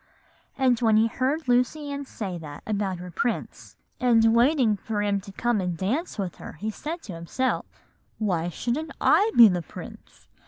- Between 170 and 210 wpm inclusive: Yes, average, 175 wpm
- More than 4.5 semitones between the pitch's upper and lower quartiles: Yes, average, 5.2 semitones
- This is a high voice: Yes, high, 225 Hz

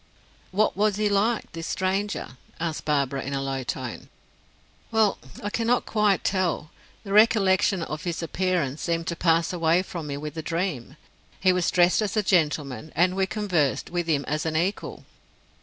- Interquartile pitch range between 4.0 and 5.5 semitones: Yes, average, 4.4 semitones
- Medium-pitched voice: Yes, medium, 175 Hz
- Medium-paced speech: Yes, average, 175 wpm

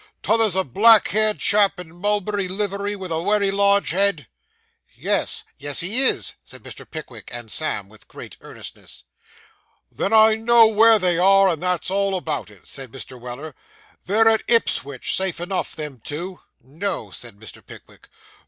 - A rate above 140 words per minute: Yes, average, 165 wpm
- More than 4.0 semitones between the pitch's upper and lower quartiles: Yes, wide, 5.4 semitones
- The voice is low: No, high, 190 Hz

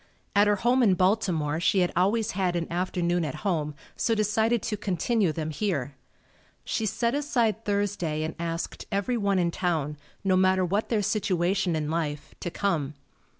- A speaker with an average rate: Yes, average, 165 wpm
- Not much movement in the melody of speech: No, average, 4.0 semitones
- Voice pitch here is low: No, medium, 185 Hz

